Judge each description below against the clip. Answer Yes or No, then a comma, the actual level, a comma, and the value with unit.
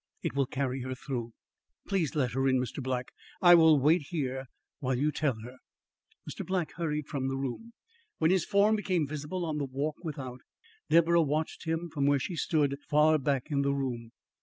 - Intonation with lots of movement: No, average, 3.5 semitones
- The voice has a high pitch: No, medium, 145 Hz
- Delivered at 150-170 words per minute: No, average, 190 wpm